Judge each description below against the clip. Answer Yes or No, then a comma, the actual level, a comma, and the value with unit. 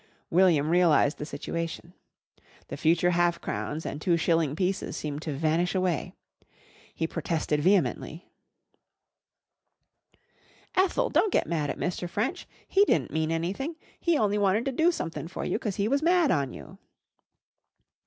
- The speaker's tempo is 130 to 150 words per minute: Yes, average, 145 wpm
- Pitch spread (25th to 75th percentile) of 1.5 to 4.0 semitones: No, average, 4.5 semitones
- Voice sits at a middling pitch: Yes, medium, 175 Hz